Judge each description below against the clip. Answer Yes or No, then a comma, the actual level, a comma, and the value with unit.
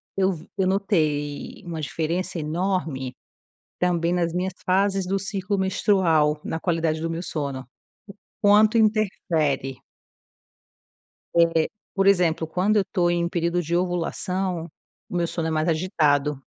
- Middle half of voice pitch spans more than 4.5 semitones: No, average, 3.1 semitones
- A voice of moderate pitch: Yes, medium, 175 Hz